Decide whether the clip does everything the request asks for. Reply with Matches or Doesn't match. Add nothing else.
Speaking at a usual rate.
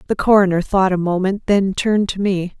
Doesn't match